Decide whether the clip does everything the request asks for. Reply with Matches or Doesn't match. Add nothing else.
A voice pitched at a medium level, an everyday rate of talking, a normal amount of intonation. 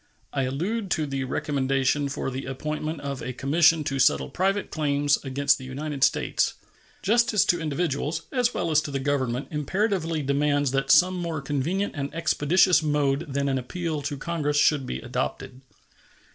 Matches